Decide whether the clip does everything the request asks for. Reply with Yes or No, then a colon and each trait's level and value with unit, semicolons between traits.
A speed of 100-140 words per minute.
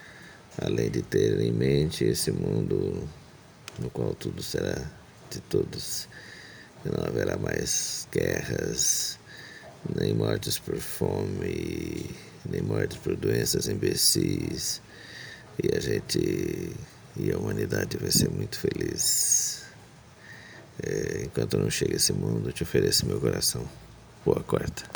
Yes: slow, 120 wpm